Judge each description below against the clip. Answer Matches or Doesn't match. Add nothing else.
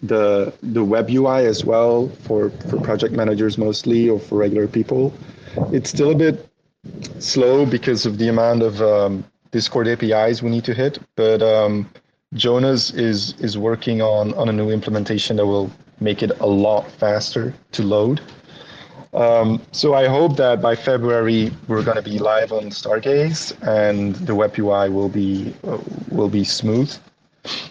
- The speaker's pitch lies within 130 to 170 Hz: Doesn't match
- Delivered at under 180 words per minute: Matches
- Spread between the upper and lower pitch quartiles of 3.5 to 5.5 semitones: Doesn't match